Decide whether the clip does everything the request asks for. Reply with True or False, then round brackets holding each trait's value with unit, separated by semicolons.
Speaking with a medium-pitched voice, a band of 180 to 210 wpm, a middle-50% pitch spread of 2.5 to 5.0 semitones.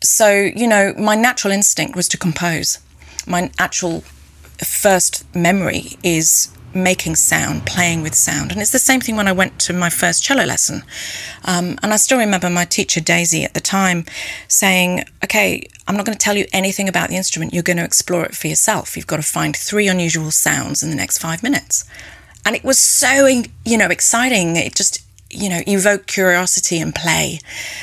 True (180 Hz; 190 wpm; 3.5 semitones)